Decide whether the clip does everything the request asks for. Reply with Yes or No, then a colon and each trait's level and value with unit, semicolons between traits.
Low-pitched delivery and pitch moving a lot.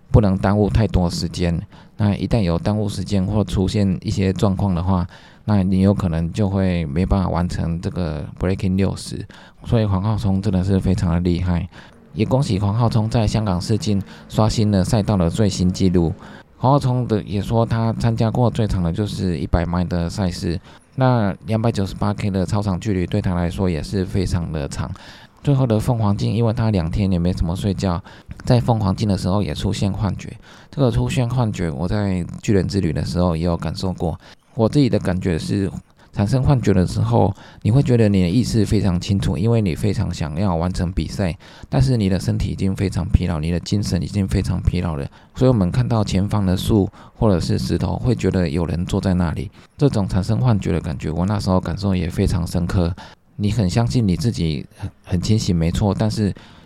No: very low, 95 Hz; average, 3.3 semitones